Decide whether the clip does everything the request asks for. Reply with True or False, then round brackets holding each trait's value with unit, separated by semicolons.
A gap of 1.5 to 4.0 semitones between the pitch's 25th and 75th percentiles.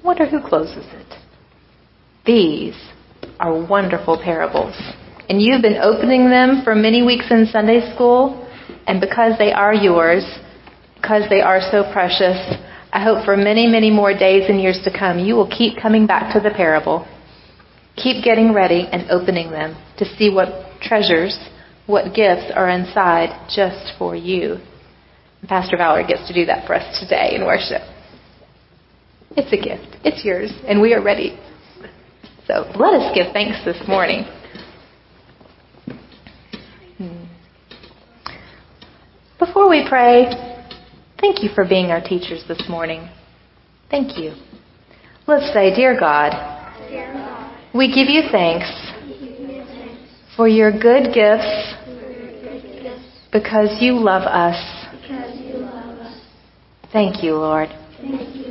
False (5.1 semitones)